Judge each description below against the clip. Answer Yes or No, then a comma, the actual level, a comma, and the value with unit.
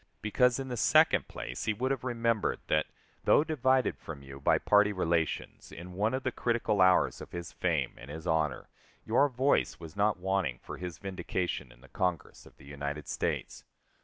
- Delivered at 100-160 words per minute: No, average, 190 wpm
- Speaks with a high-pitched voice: No, very low, 95 Hz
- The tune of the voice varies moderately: No, wide, 6.6 semitones